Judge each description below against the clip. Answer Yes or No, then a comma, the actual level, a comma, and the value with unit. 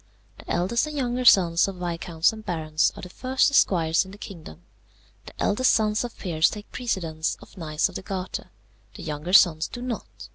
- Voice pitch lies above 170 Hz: Yes, medium, 185 Hz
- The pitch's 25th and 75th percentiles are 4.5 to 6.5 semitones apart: Yes, average, 5.2 semitones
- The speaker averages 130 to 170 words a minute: No, average, 190 wpm